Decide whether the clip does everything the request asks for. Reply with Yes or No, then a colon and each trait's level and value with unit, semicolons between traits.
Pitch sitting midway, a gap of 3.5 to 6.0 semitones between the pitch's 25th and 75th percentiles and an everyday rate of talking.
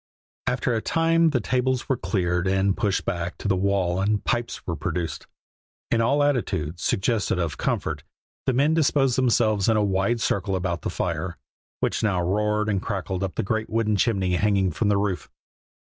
No: low, 100 Hz; average, 4.2 semitones; average, 180 wpm